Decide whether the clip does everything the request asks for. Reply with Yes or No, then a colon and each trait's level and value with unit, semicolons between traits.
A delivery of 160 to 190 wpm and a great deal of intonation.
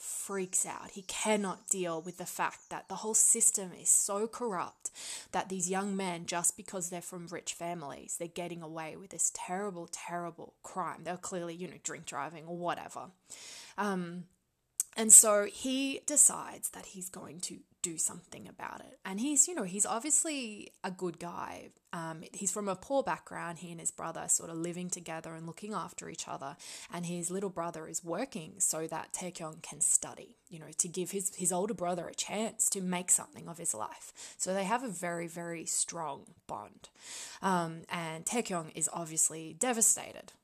No: average, 185 wpm; average, 3.4 semitones